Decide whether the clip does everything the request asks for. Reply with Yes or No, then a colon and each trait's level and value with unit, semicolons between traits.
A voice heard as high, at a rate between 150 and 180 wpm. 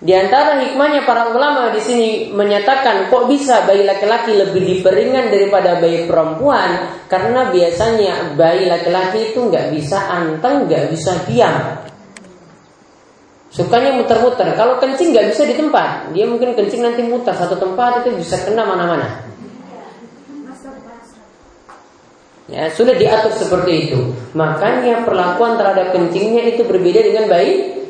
No: high, 215 Hz; average, 130 wpm